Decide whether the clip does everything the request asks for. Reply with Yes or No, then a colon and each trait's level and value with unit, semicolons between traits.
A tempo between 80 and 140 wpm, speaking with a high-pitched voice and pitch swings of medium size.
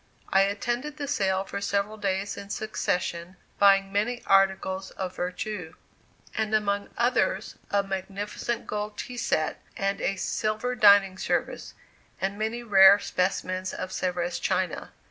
No: slow, 135 wpm; high, 200 Hz; narrow, 2.1 semitones